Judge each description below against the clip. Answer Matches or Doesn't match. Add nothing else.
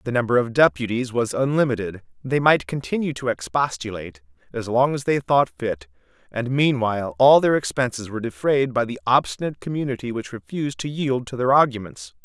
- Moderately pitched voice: Doesn't match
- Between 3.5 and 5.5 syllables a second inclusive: Doesn't match